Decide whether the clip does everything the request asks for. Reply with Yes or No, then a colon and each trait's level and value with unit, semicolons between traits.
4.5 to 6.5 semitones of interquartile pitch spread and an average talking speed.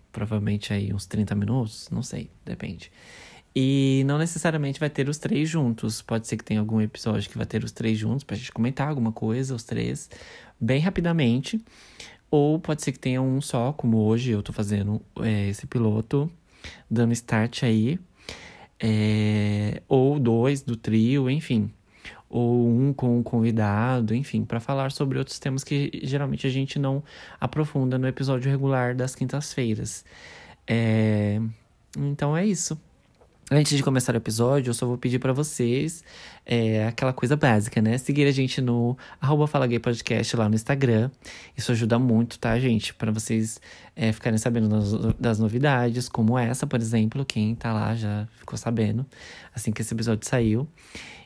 No: average, 3.6 semitones; average, 160 wpm